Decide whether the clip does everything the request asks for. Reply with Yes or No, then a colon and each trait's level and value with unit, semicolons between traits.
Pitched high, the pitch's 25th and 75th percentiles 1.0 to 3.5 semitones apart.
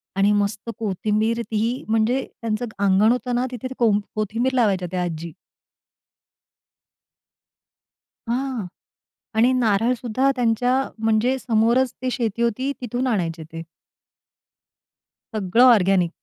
Yes: high, 225 Hz; average, 3.2 semitones